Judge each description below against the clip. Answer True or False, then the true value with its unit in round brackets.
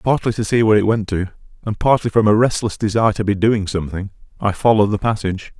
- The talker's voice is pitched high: False (105 Hz)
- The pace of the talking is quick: True (225 wpm)